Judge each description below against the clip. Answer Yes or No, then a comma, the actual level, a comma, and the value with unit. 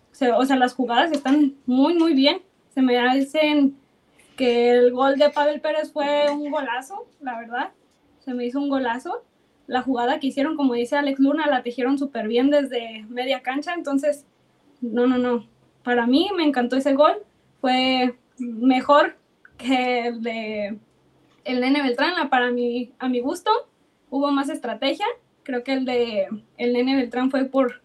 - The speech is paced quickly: No, average, 170 wpm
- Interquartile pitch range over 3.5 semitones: No, average, 3.0 semitones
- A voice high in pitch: Yes, very high, 265 Hz